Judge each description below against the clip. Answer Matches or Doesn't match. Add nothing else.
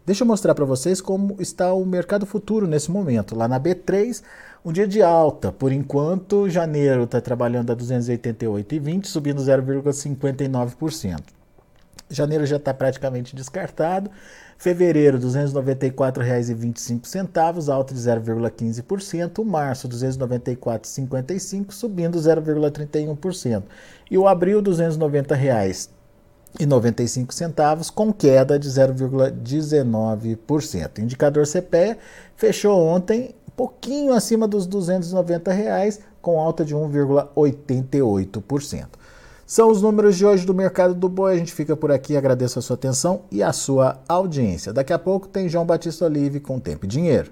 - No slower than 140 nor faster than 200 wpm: Doesn't match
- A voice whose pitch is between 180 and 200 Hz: Doesn't match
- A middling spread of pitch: Doesn't match